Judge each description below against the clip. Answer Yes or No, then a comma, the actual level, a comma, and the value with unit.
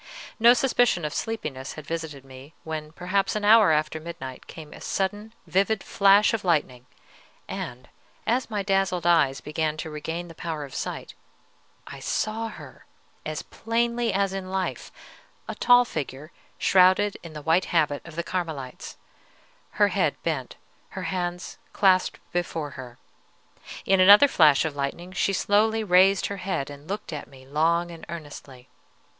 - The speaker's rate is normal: Yes, average, 155 wpm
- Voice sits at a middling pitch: Yes, medium, 175 Hz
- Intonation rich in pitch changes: No, average, 4.7 semitones